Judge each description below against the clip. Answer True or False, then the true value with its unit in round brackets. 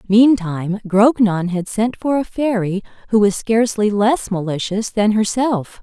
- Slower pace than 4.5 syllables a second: True (4.3 syllables/s)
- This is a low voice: False (210 Hz)